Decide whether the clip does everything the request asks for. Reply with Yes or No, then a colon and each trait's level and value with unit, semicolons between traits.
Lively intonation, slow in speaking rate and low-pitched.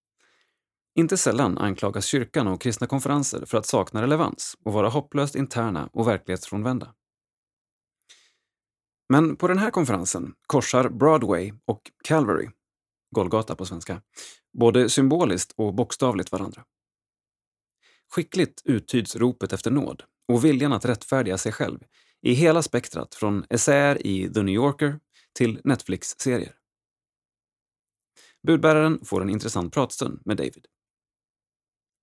Yes: wide, 5.7 semitones; slow, 120 wpm; low, 115 Hz